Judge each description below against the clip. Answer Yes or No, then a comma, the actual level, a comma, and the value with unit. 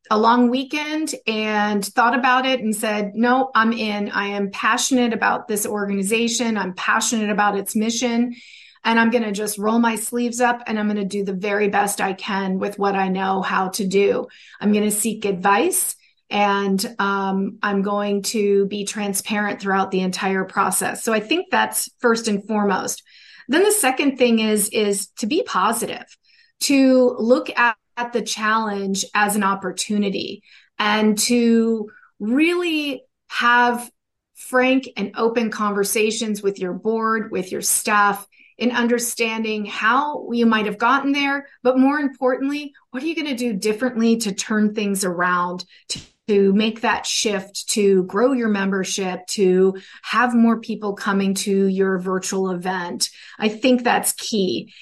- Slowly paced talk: No, average, 160 wpm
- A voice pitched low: No, high, 215 Hz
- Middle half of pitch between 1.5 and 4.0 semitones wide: Yes, average, 3.2 semitones